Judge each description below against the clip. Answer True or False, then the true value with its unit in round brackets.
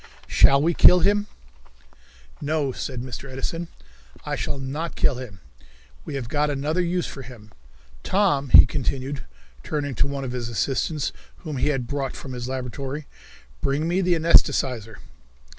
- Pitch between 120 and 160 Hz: True (140 Hz)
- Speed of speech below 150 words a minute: False (155 wpm)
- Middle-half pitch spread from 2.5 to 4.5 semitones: True (3.4 semitones)